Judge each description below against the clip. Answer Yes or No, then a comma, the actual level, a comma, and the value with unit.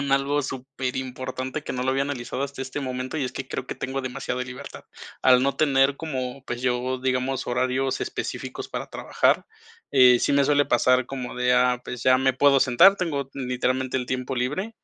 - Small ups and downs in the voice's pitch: Yes, narrow, 1.4 semitones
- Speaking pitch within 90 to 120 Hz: No, low, 130 Hz